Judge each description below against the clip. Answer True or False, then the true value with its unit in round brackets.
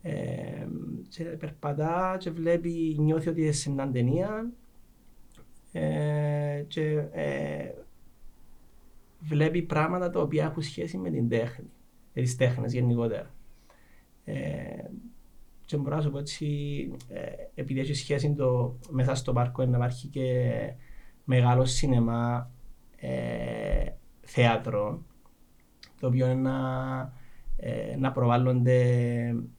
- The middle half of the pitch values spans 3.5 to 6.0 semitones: True (3.9 semitones)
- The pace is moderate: False (110 wpm)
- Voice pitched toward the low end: True (130 Hz)